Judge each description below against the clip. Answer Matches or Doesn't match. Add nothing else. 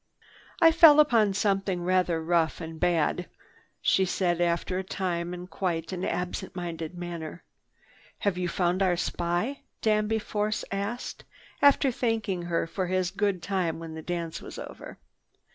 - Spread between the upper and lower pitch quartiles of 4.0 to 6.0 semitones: Doesn't match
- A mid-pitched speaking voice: Matches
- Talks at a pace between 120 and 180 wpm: Matches